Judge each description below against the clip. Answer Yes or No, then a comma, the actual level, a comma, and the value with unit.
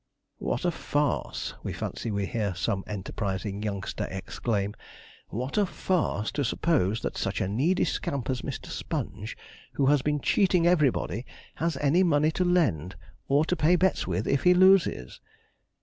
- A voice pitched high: No, medium, 140 Hz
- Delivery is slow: No, average, 160 wpm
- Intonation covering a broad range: Yes, wide, 8.8 semitones